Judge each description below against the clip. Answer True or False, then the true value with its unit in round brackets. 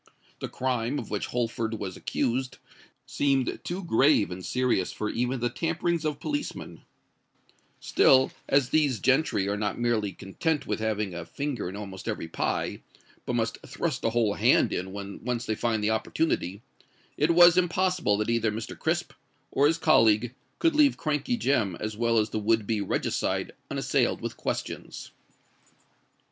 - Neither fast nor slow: True (160 wpm)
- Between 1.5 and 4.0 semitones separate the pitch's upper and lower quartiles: False (5.5 semitones)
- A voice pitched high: False (120 Hz)